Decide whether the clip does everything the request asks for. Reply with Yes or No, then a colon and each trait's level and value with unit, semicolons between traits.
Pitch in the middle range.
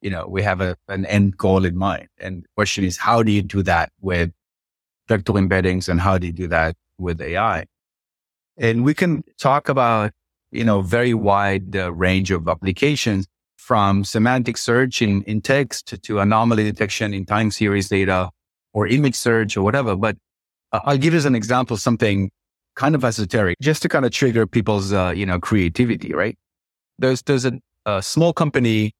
No: low, 105 Hz